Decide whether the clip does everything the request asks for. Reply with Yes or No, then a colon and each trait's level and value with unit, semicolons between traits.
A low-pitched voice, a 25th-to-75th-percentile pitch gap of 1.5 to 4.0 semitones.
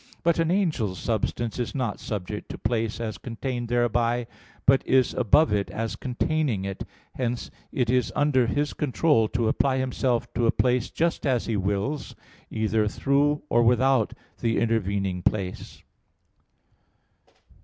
Yes: low, 120 Hz; average, 3.3 semitones